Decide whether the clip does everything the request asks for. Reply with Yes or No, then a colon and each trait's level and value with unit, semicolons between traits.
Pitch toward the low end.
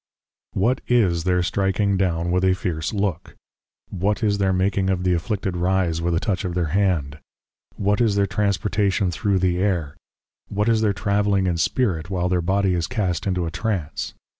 Yes: very low, 95 Hz